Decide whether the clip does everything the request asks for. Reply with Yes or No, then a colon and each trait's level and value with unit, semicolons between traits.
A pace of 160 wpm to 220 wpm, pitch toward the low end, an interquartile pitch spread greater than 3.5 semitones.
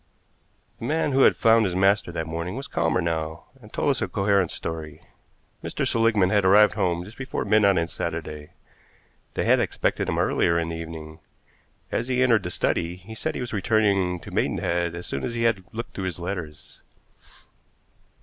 Yes: average, 190 wpm; very low, 95 Hz; average, 4.6 semitones